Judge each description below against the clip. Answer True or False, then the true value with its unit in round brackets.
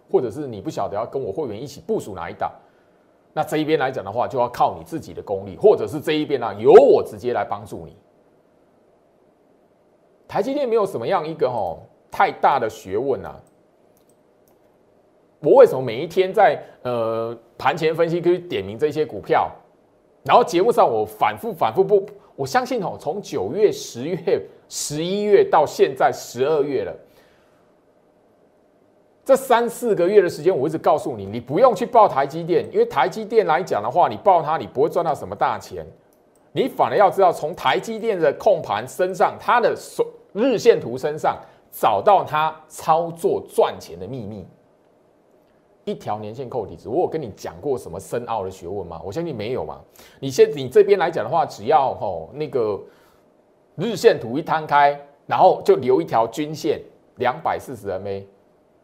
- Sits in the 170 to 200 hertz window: True (190 Hz)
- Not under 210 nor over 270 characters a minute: True (260 characters per minute)